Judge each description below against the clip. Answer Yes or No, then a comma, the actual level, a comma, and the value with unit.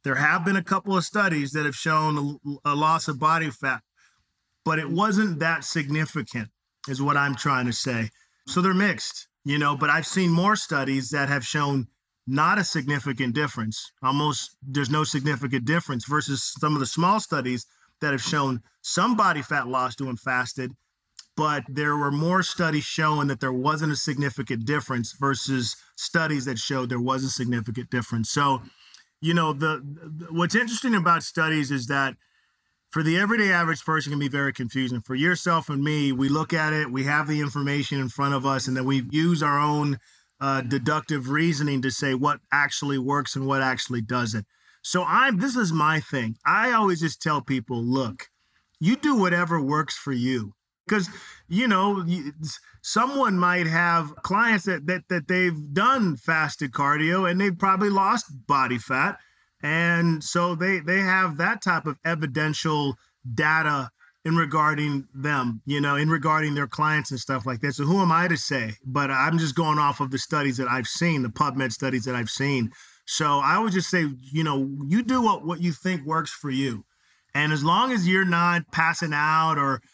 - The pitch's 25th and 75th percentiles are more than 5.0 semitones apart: No, average, 3.7 semitones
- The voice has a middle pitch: Yes, medium, 150 Hz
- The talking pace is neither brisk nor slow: Yes, average, 185 wpm